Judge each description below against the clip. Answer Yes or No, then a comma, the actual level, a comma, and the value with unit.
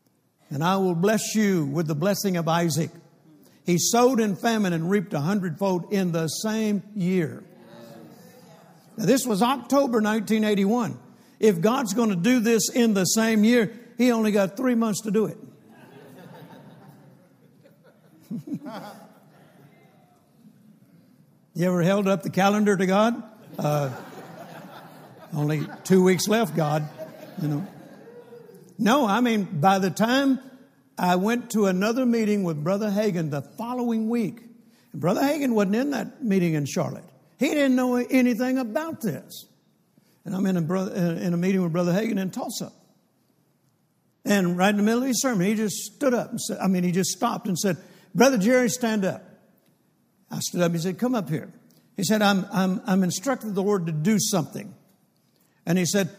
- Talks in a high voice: Yes, high, 205 Hz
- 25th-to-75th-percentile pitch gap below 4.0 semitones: No, average, 4.3 semitones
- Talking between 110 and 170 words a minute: Yes, average, 165 wpm